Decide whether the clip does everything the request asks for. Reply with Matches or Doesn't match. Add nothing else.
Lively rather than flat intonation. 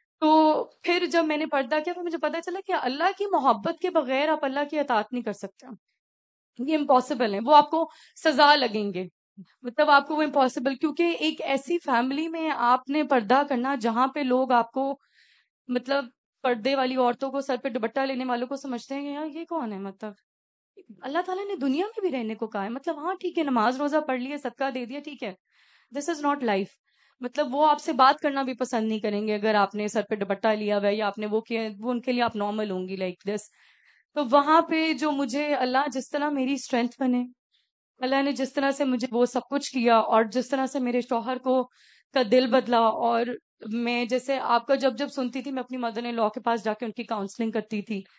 Doesn't match